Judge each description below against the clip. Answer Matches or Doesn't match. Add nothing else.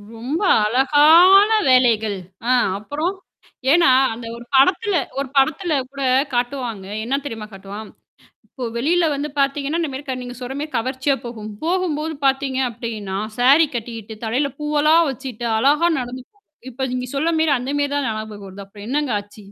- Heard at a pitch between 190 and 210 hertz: Doesn't match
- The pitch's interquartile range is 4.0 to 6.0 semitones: Matches